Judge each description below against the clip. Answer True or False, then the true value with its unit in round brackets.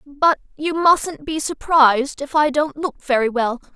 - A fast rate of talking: False (175 wpm)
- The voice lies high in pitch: True (290 Hz)